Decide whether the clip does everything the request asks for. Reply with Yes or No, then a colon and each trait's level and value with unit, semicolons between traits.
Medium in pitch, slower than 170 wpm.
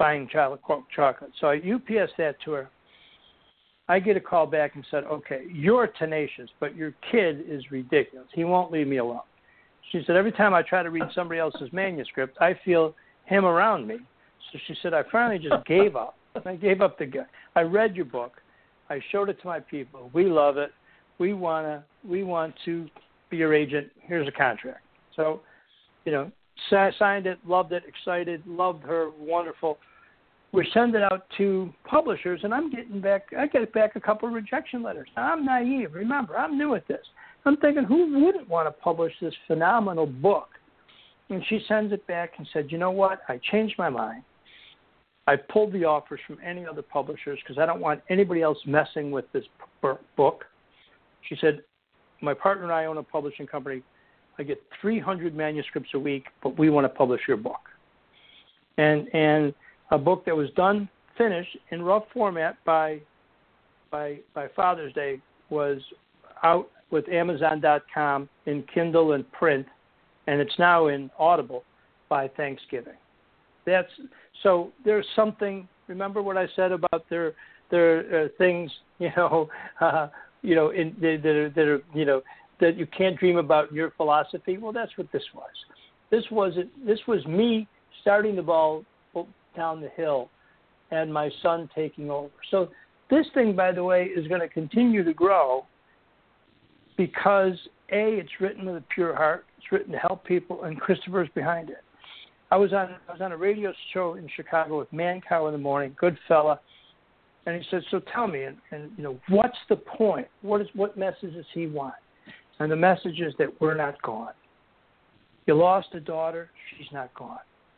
No: medium, 170 Hz; average, 175 wpm